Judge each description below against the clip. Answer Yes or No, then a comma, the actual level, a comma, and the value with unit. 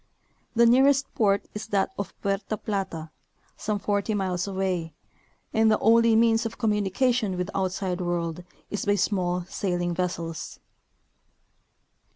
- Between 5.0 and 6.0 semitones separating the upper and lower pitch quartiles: No, average, 3.4 semitones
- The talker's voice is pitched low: No, high, 200 Hz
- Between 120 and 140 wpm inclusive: Yes, slow, 135 wpm